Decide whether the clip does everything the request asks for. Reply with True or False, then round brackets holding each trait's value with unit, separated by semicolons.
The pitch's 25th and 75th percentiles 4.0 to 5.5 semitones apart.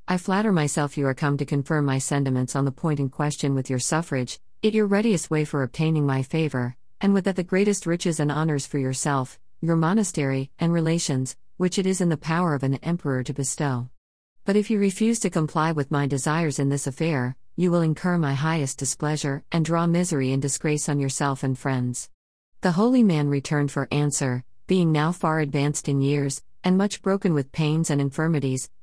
False (3.6 semitones)